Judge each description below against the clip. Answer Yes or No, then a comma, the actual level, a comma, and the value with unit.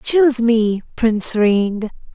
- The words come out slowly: Yes, slow, 110 wpm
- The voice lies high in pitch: Yes, high, 230 Hz